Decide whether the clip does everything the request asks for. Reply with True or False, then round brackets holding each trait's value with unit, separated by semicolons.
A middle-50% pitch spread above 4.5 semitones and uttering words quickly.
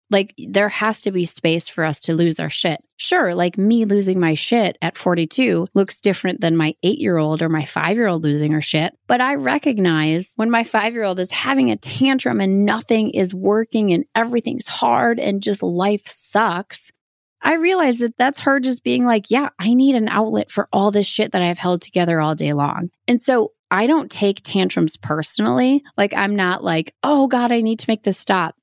True (5.3 semitones; 215 wpm)